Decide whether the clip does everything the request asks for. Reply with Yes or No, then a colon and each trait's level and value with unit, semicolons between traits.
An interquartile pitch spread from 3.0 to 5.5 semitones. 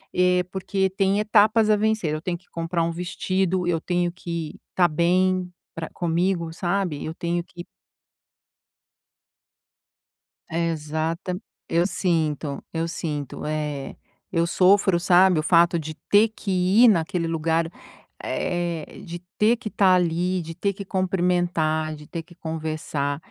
No: narrow, 2.4 semitones